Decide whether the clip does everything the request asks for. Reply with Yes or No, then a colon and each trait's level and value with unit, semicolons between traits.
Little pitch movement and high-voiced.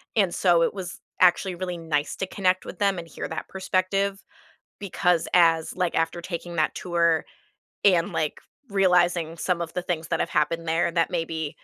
No: narrow, 2.0 semitones; medium, 175 Hz